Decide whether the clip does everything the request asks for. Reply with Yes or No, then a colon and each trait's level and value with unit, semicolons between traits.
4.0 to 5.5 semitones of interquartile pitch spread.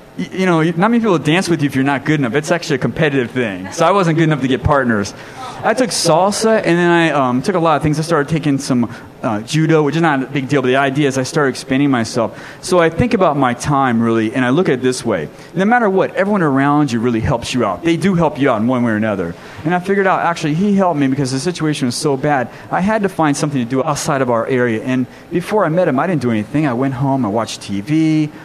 Yes: average, 4.4 semitones